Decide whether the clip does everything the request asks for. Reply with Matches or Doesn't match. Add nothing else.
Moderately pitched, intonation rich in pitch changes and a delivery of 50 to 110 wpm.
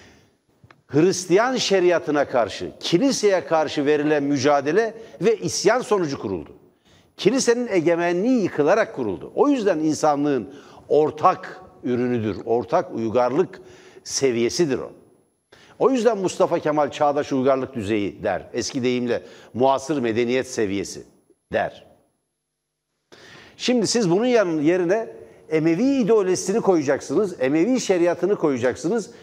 Matches